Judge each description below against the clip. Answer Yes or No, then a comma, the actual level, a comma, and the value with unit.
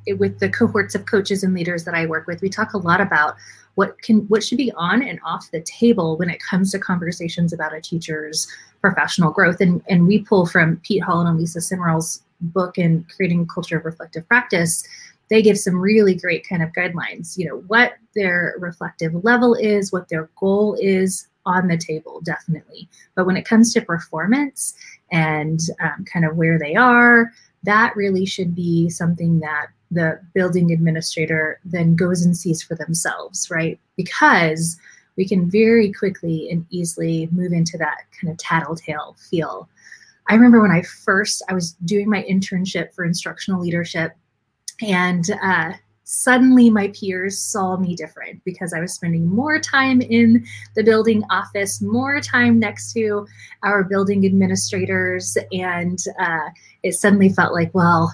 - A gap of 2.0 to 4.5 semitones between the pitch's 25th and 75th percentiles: Yes, average, 3.4 semitones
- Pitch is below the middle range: No, medium, 180 Hz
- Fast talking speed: No, average, 170 wpm